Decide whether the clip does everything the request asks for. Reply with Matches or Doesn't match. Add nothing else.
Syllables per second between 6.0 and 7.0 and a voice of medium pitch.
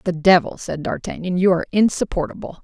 Matches